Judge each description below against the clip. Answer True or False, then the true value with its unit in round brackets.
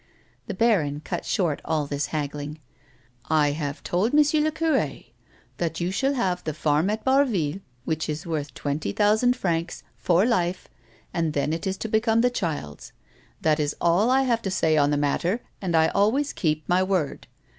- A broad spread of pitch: True (6.4 semitones)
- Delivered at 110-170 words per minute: False (185 wpm)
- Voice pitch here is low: False (170 Hz)